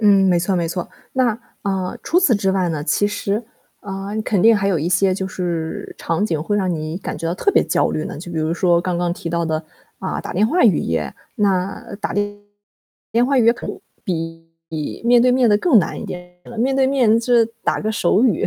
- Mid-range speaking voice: No, high, 195 Hz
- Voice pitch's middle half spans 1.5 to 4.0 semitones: No, average, 4.4 semitones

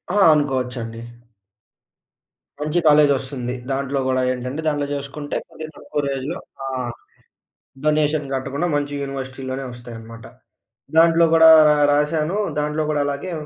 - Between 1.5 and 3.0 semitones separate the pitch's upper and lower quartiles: Yes, narrow, 2.5 semitones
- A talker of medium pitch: Yes, medium, 145 Hz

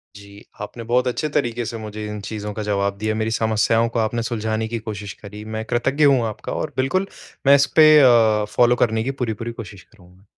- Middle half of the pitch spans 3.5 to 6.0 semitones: No, narrow, 2.4 semitones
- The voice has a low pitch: Yes, low, 110 Hz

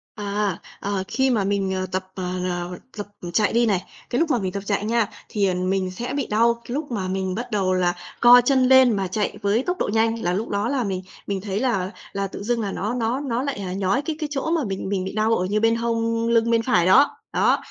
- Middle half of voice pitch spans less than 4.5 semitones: Yes, average, 3.9 semitones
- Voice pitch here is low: No, high, 215 Hz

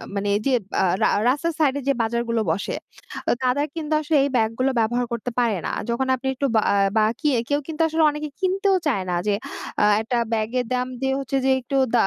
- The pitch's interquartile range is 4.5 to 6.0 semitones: No, average, 4.1 semitones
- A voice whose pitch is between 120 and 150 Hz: No, very high, 255 Hz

